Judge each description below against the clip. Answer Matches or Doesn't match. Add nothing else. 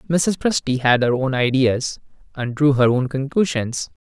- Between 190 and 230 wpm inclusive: Doesn't match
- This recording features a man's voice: Matches